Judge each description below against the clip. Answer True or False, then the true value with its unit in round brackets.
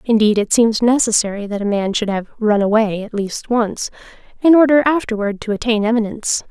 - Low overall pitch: False (220 Hz)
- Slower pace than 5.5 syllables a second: False (5.6 syllables/s)